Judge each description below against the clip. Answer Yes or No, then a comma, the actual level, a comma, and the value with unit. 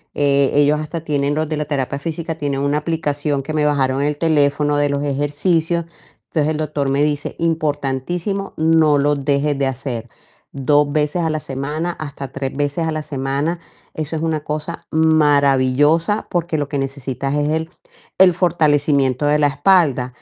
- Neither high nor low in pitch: Yes, medium, 145 Hz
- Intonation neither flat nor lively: No, narrow, 2.1 semitones